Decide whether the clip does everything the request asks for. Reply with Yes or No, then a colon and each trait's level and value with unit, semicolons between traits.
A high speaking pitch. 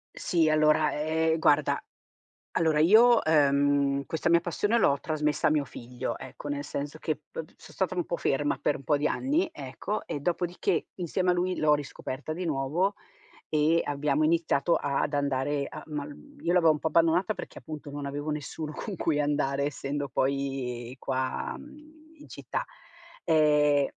No: medium, 150 Hz